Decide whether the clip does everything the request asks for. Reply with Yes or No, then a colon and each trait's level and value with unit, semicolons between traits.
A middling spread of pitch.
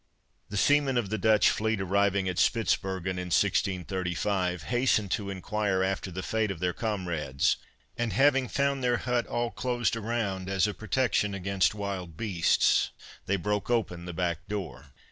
Yes: average, 3.6 semitones